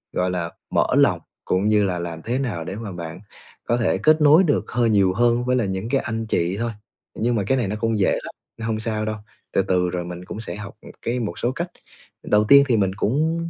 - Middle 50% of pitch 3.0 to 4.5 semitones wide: Yes, average, 4.2 semitones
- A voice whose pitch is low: Yes, low, 110 Hz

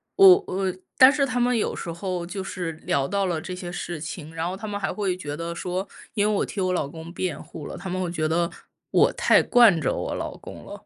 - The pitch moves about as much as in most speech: Yes, average, 3.3 semitones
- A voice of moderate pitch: Yes, medium, 180 Hz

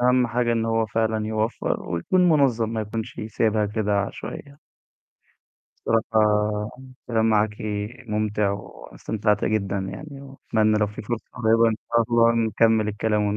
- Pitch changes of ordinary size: No, narrow, 1.7 semitones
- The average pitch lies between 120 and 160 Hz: No, low, 110 Hz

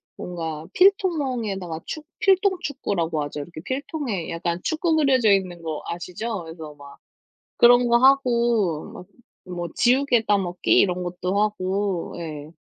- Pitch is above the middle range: Yes, high, 195 Hz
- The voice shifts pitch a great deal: Yes, wide, 7.0 semitones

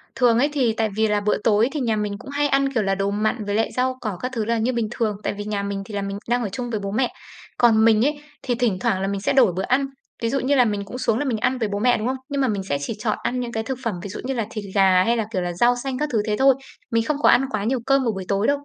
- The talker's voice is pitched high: Yes, high, 225 Hz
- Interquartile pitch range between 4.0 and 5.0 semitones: No, average, 3.6 semitones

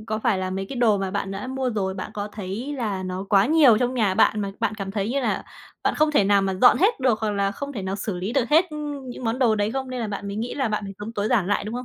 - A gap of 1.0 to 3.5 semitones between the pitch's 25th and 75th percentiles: No, average, 4.3 semitones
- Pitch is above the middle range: Yes, high, 215 Hz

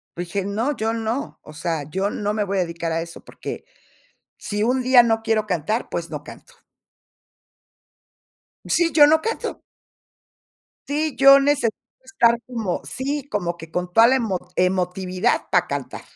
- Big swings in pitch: Yes, wide, 6.4 semitones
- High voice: Yes, high, 215 Hz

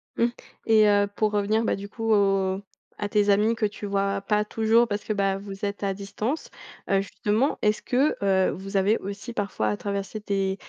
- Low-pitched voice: No, high, 205 Hz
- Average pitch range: No, narrow, 1.6 semitones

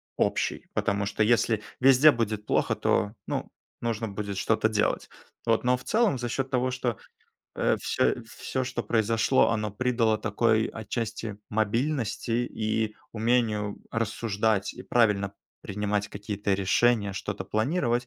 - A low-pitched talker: Yes, low, 110 Hz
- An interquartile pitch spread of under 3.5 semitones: Yes, narrow, 2.6 semitones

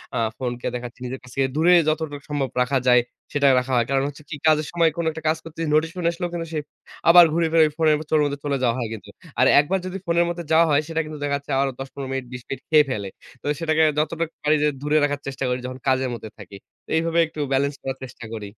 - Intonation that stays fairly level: No, average, 3.5 semitones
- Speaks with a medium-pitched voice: Yes, medium, 145 Hz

